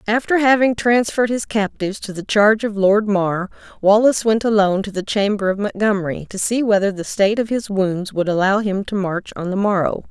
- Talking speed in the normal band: No, fast, 210 wpm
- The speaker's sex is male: No, female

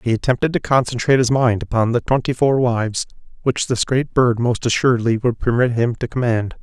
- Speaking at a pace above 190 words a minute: Yes, average, 200 wpm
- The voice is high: No, low, 120 Hz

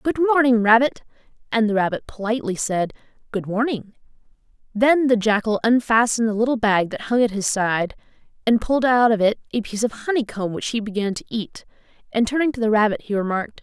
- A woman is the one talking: Yes, female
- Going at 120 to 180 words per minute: No, average, 190 wpm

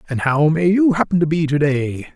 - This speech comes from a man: Yes, male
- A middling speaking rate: No, fast, 250 wpm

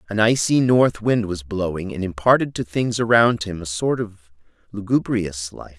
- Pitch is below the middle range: Yes, low, 105 Hz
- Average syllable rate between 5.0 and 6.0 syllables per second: No, 4.6 syllables/s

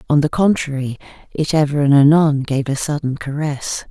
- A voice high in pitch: No, medium, 145 Hz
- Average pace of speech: Yes, average, 170 wpm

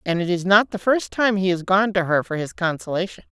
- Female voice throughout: Yes, female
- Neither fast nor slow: No, fast, 270 wpm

